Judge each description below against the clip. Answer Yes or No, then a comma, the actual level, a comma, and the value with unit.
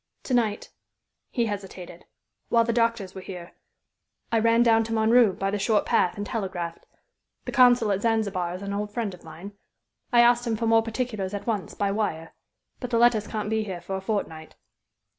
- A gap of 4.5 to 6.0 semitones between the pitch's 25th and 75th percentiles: No, average, 3.2 semitones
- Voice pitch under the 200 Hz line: No, high, 210 Hz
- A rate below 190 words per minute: No, average, 195 wpm